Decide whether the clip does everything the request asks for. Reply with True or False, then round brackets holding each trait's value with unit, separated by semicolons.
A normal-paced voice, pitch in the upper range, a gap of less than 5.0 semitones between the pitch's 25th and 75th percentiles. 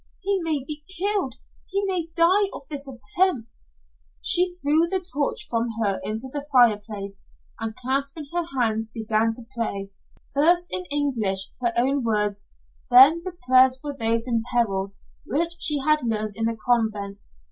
False (160 wpm; 255 Hz; 5.6 semitones)